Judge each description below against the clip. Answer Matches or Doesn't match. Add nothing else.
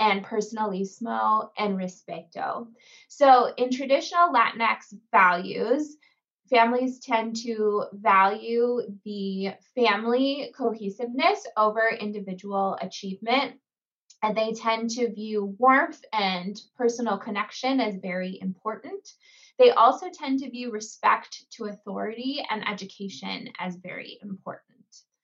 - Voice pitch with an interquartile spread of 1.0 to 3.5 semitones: Doesn't match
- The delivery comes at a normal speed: Doesn't match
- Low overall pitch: Doesn't match